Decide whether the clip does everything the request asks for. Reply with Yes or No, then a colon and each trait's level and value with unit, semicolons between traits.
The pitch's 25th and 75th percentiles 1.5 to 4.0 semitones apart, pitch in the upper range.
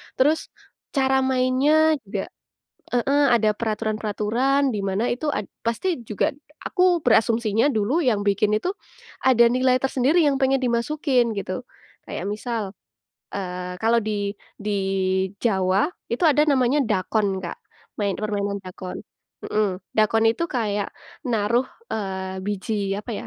No: average, 4.5 semitones; high, 225 Hz